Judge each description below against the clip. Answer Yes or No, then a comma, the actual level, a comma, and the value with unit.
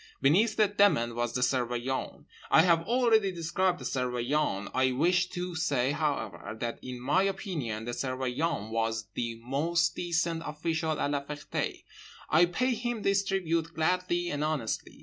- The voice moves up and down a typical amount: No, wide, 6.1 semitones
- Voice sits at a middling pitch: Yes, medium, 155 Hz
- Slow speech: No, average, 155 wpm